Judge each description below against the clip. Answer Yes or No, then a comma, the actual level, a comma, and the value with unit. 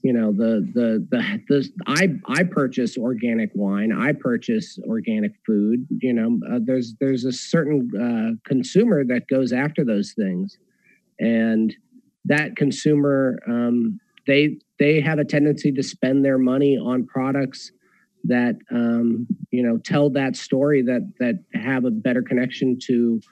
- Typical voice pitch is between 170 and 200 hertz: No, low, 135 Hz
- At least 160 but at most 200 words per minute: No, average, 150 wpm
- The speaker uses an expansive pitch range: Yes, wide, 7.6 semitones